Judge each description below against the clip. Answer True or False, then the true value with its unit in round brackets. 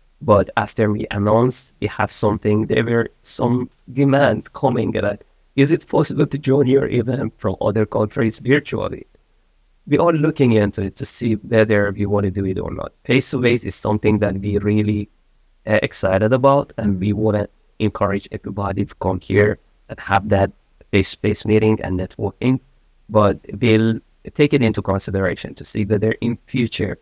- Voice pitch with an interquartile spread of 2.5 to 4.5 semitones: True (3.3 semitones)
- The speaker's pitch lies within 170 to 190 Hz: False (110 Hz)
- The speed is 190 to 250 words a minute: False (175 wpm)